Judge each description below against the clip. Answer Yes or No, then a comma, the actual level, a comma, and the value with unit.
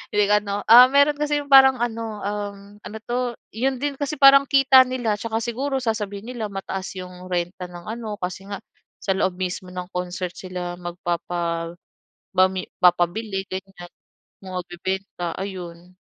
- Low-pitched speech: No, high, 200 Hz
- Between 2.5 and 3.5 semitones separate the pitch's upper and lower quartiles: No, average, 4.7 semitones